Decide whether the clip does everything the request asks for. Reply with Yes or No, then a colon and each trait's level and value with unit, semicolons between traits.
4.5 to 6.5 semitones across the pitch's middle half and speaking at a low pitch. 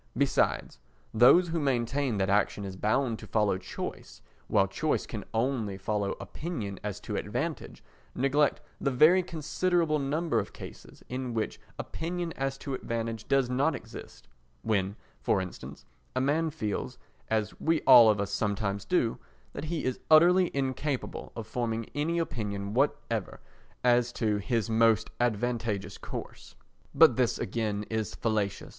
Yes: average, 5.3 semitones; low, 120 Hz